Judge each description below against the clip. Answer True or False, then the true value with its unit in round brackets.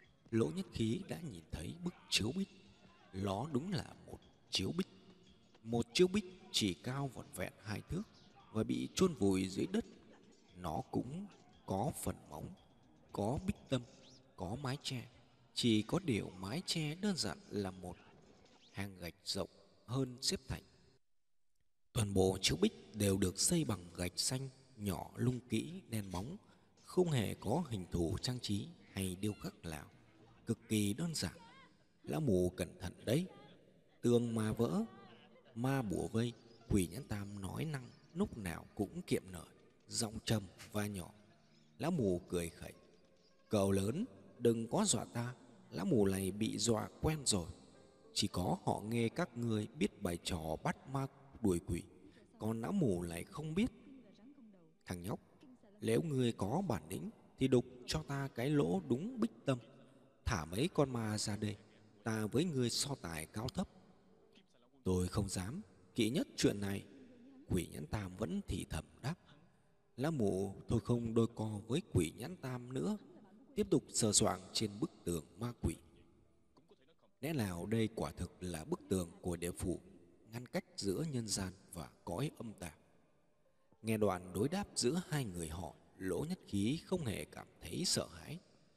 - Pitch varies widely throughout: True (6.2 semitones)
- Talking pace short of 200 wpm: True (165 wpm)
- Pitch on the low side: True (115 Hz)